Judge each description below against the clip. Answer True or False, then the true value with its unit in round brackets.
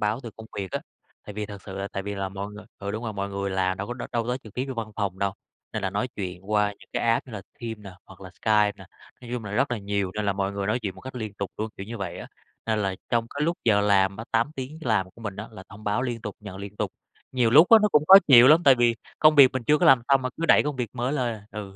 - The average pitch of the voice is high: False (105 Hz)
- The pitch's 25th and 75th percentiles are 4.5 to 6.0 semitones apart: False (3.5 semitones)